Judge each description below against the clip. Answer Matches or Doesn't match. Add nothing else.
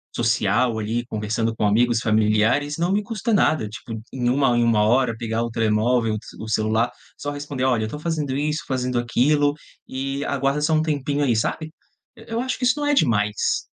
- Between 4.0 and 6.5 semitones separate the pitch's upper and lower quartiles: Matches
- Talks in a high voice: Doesn't match